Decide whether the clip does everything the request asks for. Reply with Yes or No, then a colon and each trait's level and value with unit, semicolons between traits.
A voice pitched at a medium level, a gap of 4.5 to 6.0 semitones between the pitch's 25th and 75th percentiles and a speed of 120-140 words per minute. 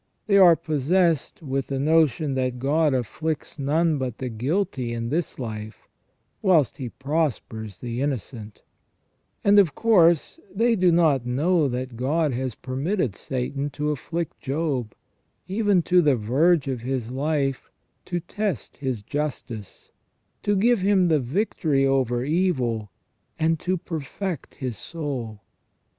Yes: medium, 145 Hz; average, 5.1 semitones; slow, 135 wpm